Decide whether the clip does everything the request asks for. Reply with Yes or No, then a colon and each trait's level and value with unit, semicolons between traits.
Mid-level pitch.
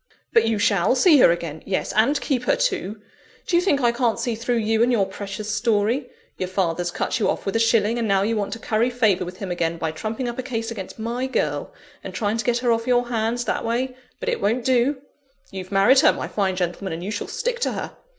No: high, 225 Hz